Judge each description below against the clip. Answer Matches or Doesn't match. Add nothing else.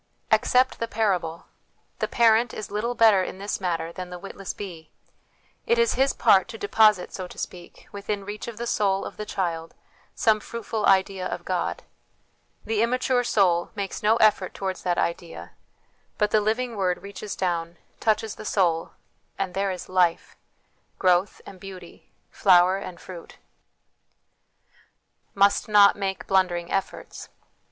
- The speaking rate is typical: Matches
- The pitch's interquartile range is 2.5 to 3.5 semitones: Matches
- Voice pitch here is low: Doesn't match